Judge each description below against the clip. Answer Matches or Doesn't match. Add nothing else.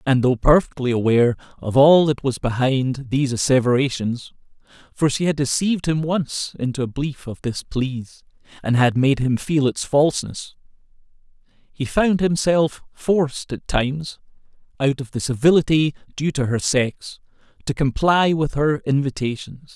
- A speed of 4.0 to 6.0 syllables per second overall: Matches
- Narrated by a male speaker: Matches